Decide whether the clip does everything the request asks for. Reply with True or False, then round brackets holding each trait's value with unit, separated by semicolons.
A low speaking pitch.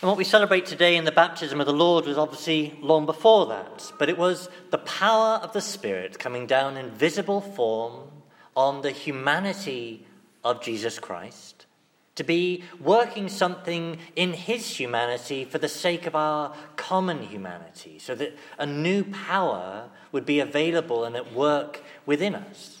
False (160 Hz)